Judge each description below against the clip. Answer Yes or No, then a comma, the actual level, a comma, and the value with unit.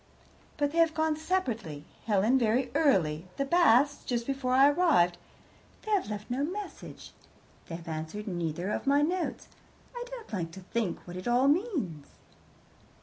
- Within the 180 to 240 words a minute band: No, average, 160 wpm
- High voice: Yes, very high, 250 Hz